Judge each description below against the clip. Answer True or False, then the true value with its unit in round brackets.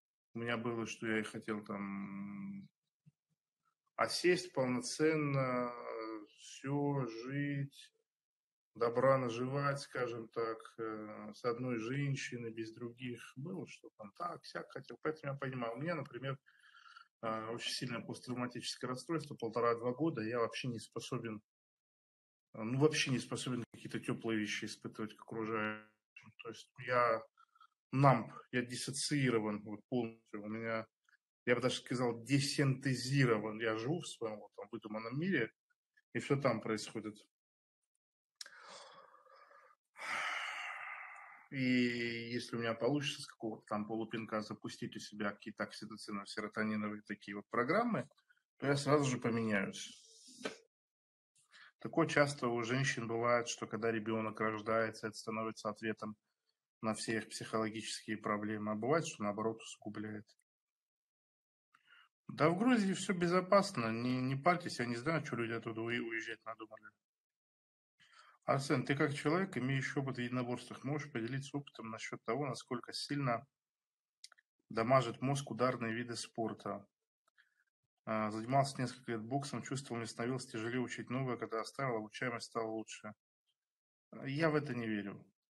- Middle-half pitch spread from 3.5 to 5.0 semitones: True (4.2 semitones)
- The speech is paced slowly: False (125 wpm)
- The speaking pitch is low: True (120 Hz)